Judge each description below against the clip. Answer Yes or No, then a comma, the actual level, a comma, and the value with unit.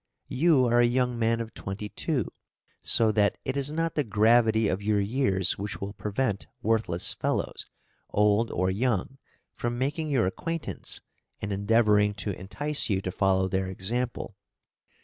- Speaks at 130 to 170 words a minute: Yes, average, 155 wpm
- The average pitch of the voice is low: Yes, low, 110 Hz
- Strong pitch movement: No, average, 3.9 semitones